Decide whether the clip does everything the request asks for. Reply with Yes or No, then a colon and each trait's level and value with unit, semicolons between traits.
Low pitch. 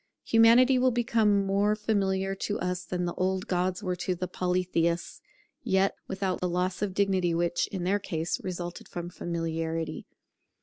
No: medium, 185 Hz